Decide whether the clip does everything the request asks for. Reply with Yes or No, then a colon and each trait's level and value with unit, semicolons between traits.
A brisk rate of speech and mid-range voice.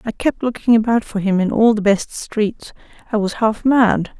No: fast, 215 wpm; high, 220 Hz